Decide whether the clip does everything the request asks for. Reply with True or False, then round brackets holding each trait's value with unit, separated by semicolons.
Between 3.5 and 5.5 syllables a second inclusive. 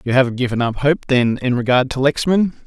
False (5.7 syllables/s)